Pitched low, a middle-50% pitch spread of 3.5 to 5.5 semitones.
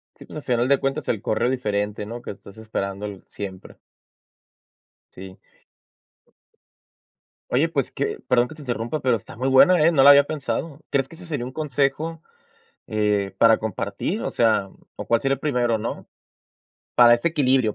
Yes: low, 125 Hz; average, 4.6 semitones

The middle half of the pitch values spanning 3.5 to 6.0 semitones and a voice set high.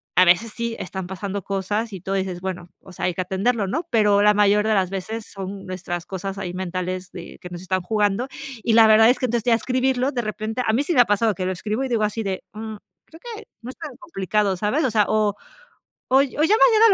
Yes: average, 3.8 semitones; high, 210 Hz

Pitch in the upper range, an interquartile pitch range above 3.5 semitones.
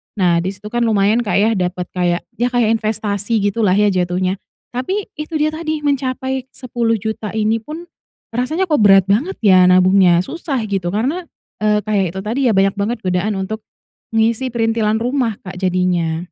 Yes: high, 215 Hz; average, 4.5 semitones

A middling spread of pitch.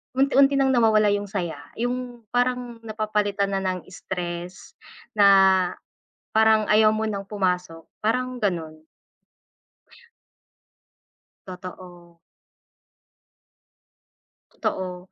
Yes: average, 3.9 semitones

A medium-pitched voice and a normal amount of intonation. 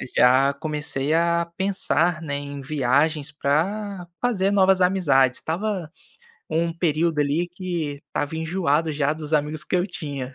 Yes: medium, 160 Hz; average, 3.7 semitones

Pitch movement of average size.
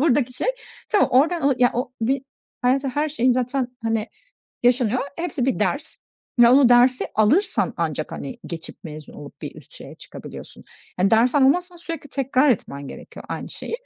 Yes: average, 3.1 semitones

